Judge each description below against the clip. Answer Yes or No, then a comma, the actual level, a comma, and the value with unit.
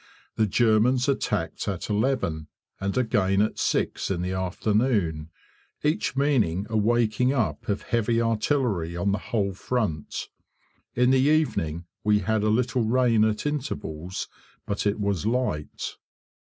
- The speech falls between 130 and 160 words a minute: Yes, average, 140 wpm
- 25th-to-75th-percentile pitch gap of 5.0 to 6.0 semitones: No, average, 4.4 semitones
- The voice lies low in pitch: Yes, low, 110 Hz